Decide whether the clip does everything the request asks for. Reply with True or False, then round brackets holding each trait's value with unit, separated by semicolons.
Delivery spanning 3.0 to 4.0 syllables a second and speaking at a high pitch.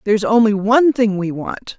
False (5.4 syllables/s; 215 Hz)